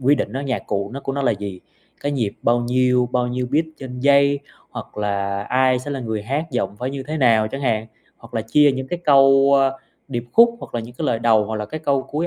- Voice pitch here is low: Yes, low, 125 Hz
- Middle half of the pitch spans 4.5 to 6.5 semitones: No, average, 3.7 semitones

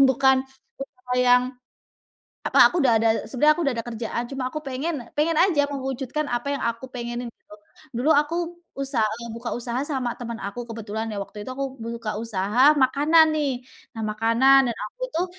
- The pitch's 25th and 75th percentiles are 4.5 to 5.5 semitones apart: No, average, 3.3 semitones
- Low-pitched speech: No, very high, 250 Hz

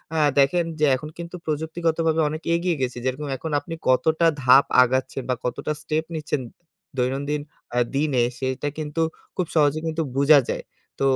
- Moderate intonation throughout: Yes, average, 3.2 semitones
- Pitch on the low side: No, medium, 150 Hz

